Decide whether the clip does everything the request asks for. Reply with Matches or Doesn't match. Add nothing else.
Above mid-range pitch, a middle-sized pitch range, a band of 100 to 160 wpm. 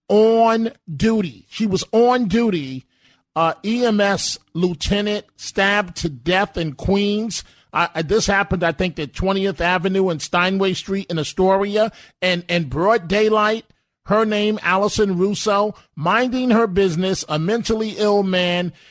Matches